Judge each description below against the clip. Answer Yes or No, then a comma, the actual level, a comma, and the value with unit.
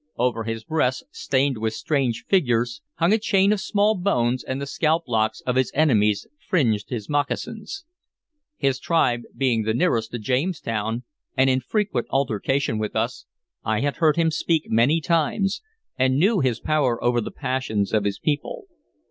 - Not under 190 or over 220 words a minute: No, average, 165 wpm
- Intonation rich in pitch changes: Yes, wide, 5.7 semitones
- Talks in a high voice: No, low, 130 Hz